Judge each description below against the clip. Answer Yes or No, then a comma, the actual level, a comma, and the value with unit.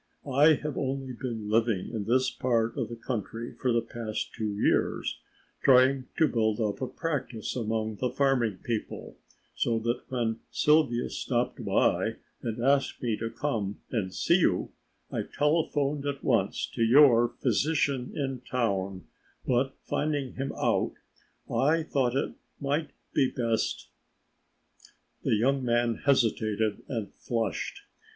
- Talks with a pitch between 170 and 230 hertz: No, low, 120 Hz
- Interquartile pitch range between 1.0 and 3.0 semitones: No, average, 3.5 semitones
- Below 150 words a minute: Yes, average, 140 wpm